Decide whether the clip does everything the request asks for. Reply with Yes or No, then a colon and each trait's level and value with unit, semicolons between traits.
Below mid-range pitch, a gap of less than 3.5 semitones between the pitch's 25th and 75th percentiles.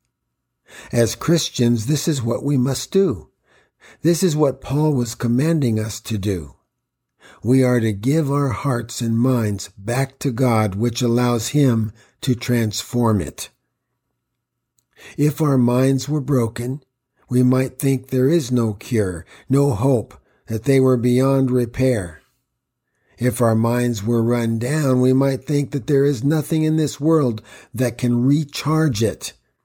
Yes: low, 125 Hz; average, 3.0 semitones